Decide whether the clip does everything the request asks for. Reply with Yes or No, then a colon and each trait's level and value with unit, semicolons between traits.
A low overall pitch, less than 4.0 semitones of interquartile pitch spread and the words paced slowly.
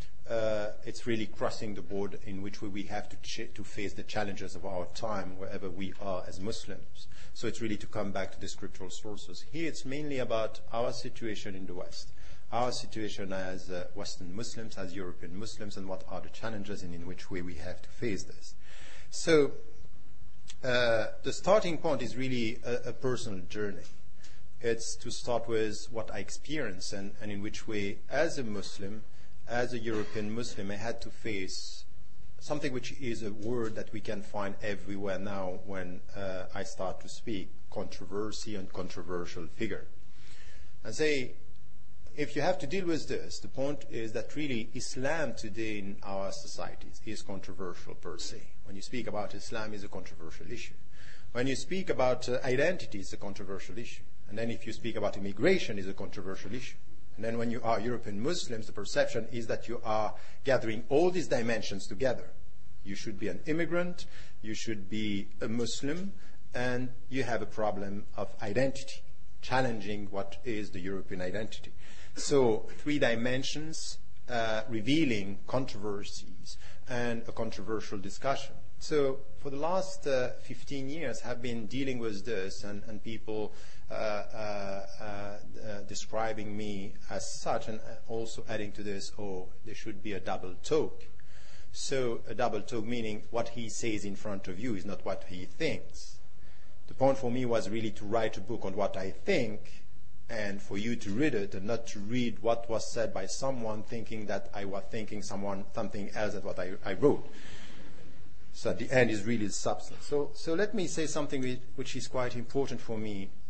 No: low, 110 Hz; average, 3.3 semitones; average, 180 wpm